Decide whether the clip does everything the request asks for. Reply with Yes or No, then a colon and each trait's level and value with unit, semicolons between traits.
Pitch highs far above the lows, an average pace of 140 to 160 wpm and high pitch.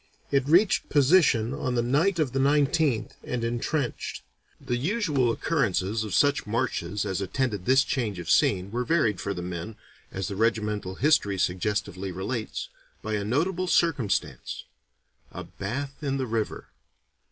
No: wide, 5.8 semitones; average, 150 wpm; low, 120 Hz